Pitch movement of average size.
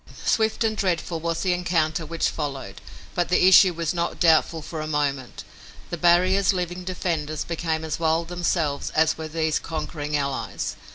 No: narrow, 2.2 semitones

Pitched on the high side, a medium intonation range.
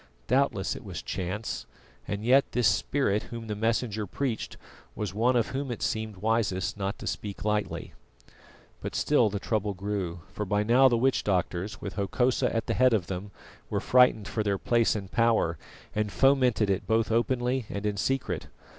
No: low, 110 Hz; average, 3.3 semitones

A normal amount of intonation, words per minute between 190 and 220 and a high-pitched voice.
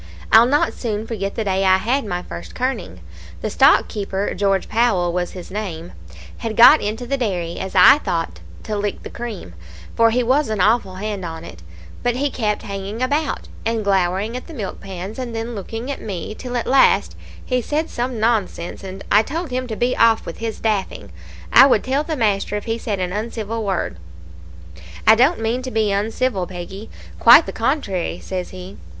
Yes: average, 4.1 semitones; average, 195 wpm; high, 215 Hz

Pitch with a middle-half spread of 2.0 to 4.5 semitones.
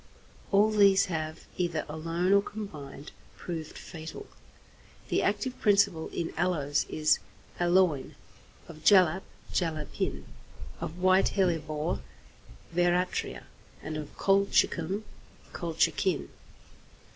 Yes: average, 3.7 semitones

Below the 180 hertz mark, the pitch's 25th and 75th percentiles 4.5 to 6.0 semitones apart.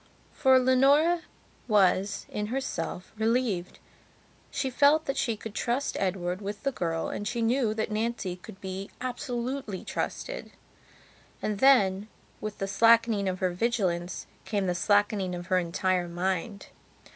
No: high, 210 Hz; average, 4.8 semitones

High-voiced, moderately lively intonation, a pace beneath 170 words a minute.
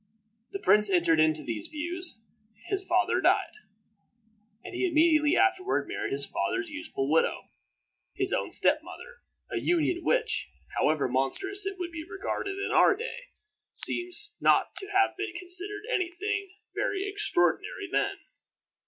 Yes: very high, 360 Hz; average, 4.2 semitones; average, 145 wpm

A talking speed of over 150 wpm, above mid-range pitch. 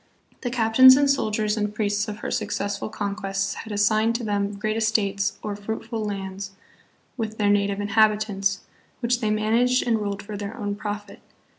Yes: average, 170 wpm; high, 210 Hz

